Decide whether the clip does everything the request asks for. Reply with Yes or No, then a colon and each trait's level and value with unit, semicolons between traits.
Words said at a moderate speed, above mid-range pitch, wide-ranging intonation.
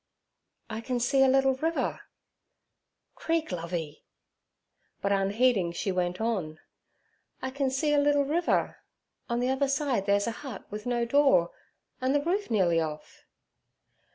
Yes: average, 145 wpm; high, 245 Hz; wide, 6.2 semitones